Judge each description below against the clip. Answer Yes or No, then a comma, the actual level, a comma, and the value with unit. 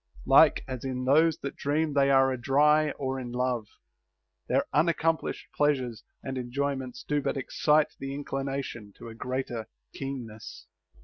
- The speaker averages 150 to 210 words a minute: No, average, 140 wpm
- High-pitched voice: No, low, 135 Hz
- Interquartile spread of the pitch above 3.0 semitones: No, narrow, 2.4 semitones